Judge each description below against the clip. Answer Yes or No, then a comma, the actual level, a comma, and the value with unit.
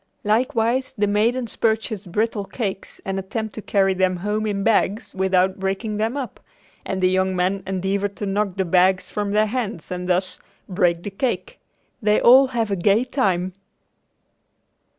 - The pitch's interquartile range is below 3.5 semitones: Yes, average, 2.8 semitones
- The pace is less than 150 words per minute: No, average, 165 wpm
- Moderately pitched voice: No, high, 200 Hz